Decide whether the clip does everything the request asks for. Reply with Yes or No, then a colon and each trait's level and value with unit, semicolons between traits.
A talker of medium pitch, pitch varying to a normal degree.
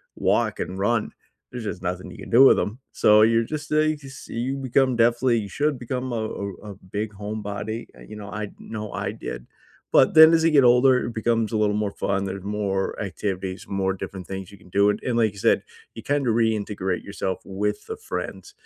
No: low, 110 Hz; average, 3.8 semitones